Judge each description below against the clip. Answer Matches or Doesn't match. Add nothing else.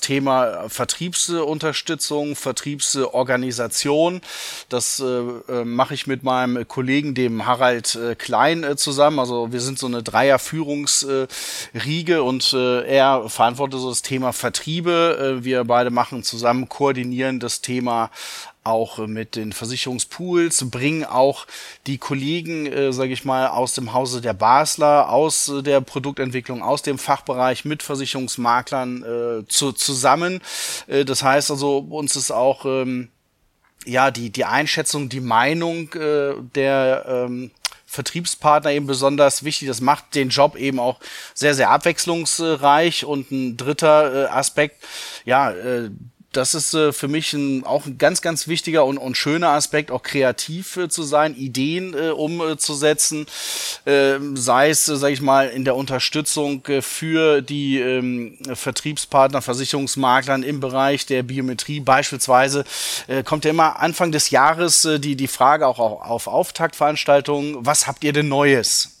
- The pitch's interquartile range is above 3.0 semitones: Doesn't match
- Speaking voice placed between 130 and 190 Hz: Matches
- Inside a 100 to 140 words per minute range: Matches